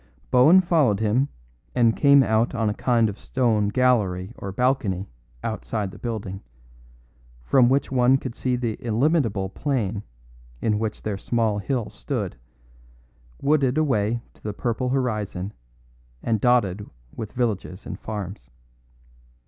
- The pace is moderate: No, slow, 130 wpm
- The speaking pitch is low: Yes, low, 115 Hz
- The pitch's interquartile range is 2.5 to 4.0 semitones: Yes, average, 3.7 semitones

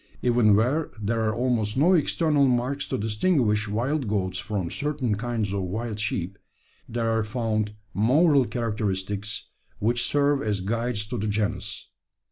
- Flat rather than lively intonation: No, average, 3.4 semitones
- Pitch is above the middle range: No, low, 110 Hz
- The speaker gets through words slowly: No, average, 145 wpm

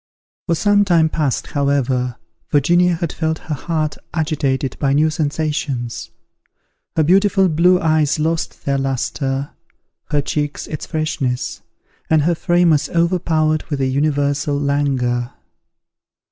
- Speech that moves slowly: Yes, slow, 125 wpm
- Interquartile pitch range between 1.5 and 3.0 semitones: Yes, average, 2.7 semitones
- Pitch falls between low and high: Yes, medium, 150 Hz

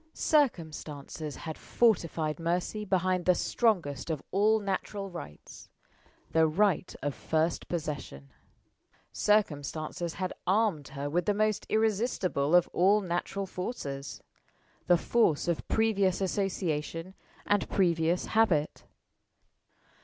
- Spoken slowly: Yes, slow, 110 wpm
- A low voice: No, medium, 180 Hz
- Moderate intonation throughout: Yes, average, 4.6 semitones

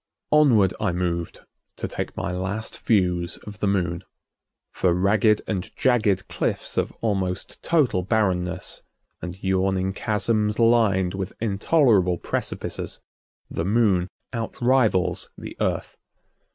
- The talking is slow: Yes, slow, 115 wpm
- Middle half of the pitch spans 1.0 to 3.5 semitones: Yes, average, 3.2 semitones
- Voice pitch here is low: Yes, very low, 95 Hz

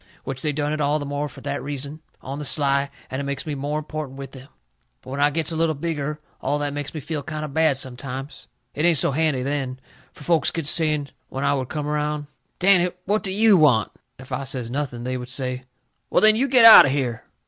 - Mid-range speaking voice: Yes, medium, 145 Hz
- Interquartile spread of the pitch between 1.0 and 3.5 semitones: Yes, narrow, 2.4 semitones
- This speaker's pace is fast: Yes, fast, 245 wpm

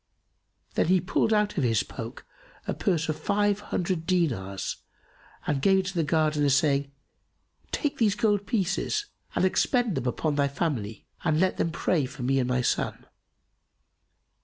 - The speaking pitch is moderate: Yes, medium, 160 Hz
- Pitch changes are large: Yes, wide, 5.9 semitones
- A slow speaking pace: No, average, 170 wpm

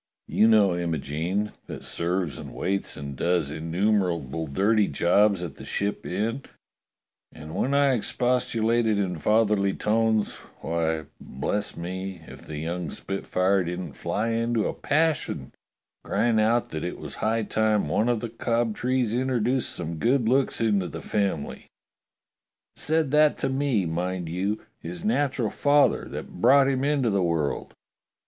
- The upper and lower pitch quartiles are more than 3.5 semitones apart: Yes, average, 5.2 semitones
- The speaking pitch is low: Yes, low, 105 Hz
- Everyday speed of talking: Yes, average, 150 wpm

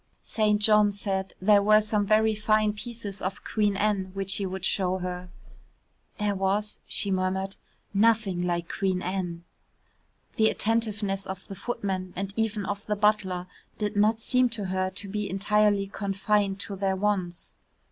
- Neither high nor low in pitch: No, high, 200 Hz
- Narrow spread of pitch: Yes, narrow, 1.8 semitones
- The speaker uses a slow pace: No, average, 155 wpm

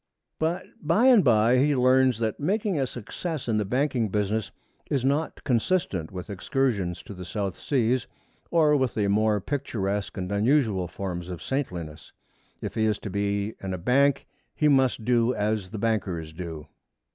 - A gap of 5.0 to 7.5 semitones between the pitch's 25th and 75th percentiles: Yes, wide, 5.5 semitones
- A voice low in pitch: Yes, low, 110 Hz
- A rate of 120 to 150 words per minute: No, average, 170 wpm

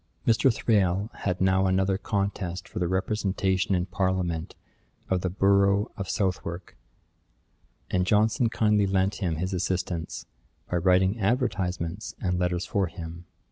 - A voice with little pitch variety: Yes, narrow, 1.8 semitones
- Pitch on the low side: Yes, very low, 95 Hz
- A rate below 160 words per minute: Yes, slow, 135 wpm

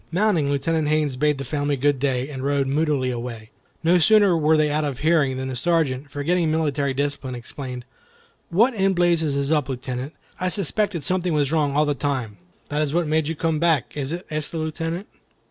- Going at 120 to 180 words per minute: No, average, 200 wpm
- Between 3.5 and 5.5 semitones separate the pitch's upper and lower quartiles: No, average, 3.1 semitones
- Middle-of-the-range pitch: Yes, medium, 150 Hz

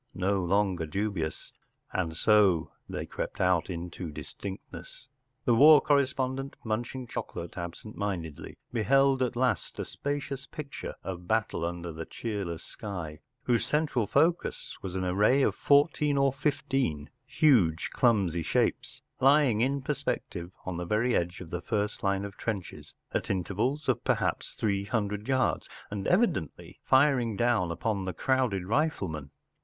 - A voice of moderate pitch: No, low, 105 Hz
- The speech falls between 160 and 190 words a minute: No, average, 140 wpm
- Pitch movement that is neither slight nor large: No, wide, 6.6 semitones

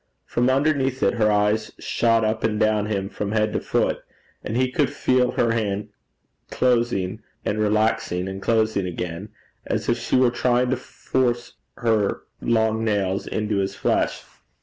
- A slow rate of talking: No, average, 160 wpm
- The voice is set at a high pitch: No, low, 110 Hz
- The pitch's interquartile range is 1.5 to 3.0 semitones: Yes, narrow, 2.6 semitones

